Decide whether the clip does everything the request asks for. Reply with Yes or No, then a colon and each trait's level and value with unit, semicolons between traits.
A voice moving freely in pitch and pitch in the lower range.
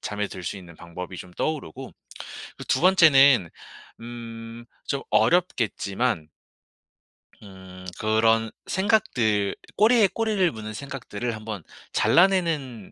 Yes: wide, 7.5 semitones; low, 115 Hz